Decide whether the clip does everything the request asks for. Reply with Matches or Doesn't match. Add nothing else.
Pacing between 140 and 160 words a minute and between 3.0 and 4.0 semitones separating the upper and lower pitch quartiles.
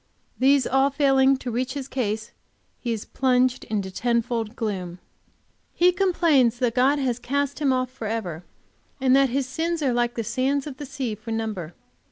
Doesn't match